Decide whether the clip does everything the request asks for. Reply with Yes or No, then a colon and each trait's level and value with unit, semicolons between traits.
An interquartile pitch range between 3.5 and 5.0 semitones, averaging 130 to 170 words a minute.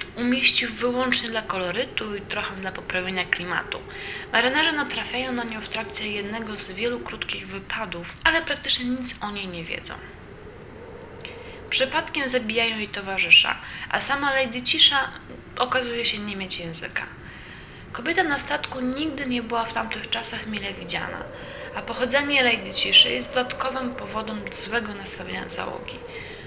Yes: average, 4.7 semitones; average, 140 wpm